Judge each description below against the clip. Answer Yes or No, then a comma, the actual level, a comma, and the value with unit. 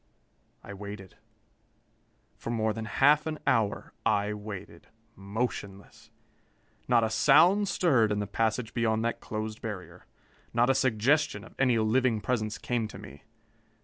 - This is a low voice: Yes, low, 110 Hz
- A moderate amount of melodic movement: Yes, average, 3.0 semitones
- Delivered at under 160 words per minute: Yes, average, 140 wpm